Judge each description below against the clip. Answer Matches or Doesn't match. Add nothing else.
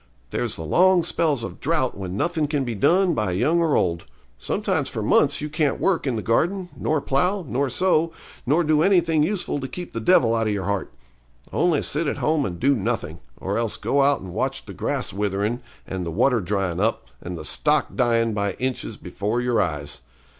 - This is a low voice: Matches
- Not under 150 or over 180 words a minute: Doesn't match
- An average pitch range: Doesn't match